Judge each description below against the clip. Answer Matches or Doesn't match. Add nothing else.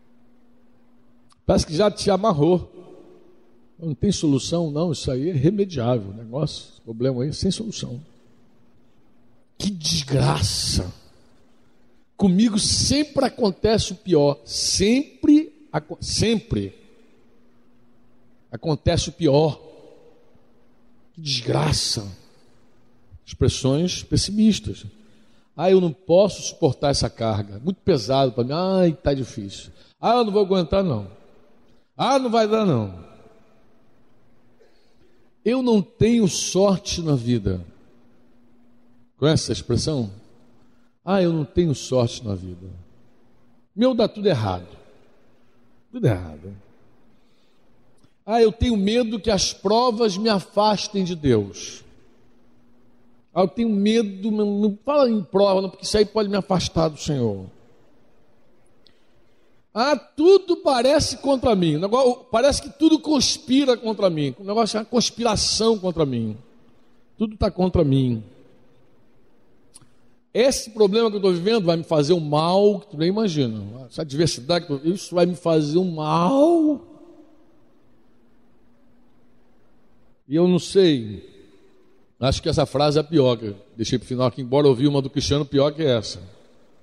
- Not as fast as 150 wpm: Matches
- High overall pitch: Doesn't match